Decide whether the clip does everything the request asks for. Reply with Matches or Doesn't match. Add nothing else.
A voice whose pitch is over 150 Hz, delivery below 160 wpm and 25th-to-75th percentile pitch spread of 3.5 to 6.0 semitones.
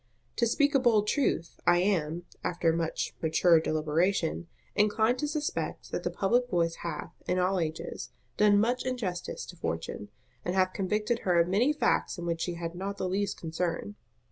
Doesn't match